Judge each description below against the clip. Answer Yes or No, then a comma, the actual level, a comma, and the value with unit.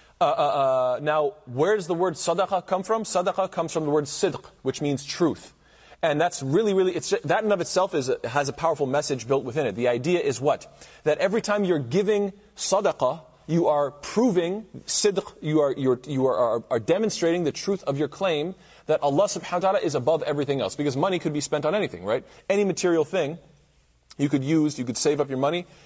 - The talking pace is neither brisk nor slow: No, fast, 220 wpm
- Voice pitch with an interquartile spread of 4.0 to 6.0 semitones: Yes, average, 4.7 semitones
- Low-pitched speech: No, medium, 165 Hz